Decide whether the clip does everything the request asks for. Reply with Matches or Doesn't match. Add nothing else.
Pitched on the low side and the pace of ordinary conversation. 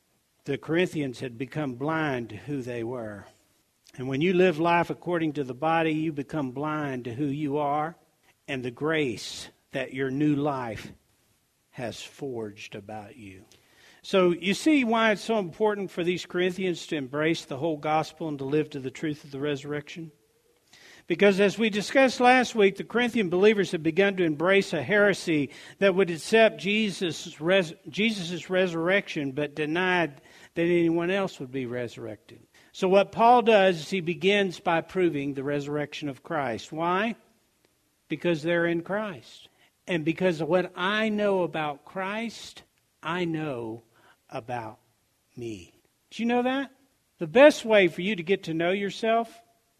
Doesn't match